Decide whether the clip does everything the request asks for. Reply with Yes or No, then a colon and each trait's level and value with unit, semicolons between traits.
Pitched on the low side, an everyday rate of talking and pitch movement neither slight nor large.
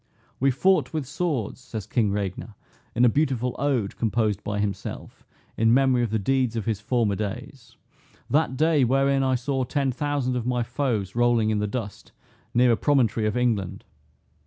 Yes: low, 120 Hz; average, 175 wpm; average, 3.7 semitones